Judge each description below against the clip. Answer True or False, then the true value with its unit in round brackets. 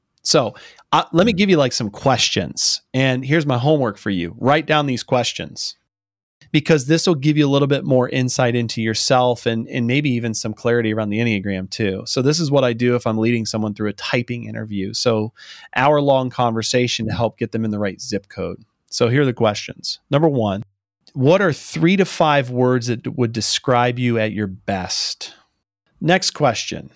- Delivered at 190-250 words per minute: True (200 wpm)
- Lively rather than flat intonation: False (4.2 semitones)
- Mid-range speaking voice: False (120 Hz)